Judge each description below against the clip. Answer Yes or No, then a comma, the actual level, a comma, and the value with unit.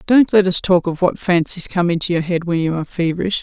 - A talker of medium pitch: Yes, medium, 175 Hz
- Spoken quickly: Yes, fast, 265 wpm